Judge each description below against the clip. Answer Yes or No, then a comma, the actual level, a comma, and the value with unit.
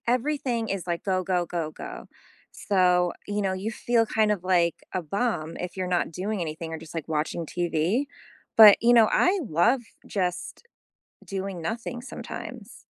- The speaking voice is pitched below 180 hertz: No, medium, 185 Hz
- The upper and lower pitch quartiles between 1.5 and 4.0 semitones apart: No, average, 4.5 semitones